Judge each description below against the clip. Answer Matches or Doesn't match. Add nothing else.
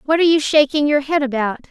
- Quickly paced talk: Matches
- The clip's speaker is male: Doesn't match